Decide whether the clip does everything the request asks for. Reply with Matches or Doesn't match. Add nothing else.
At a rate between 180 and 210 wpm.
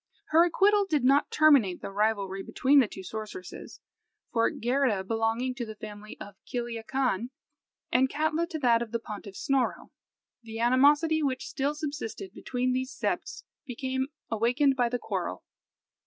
Doesn't match